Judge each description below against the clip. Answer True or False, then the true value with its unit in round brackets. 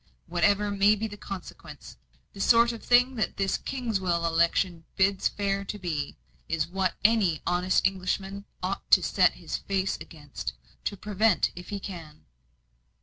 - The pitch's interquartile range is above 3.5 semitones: False (2.9 semitones)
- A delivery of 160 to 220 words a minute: False (150 wpm)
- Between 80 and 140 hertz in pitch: False (195 Hz)